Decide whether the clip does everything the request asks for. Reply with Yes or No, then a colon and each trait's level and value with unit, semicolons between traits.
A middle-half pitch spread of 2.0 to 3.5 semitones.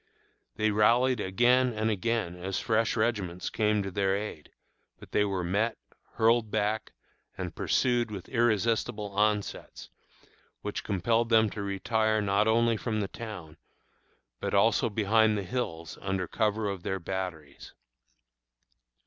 Yes: narrow, 2.6 semitones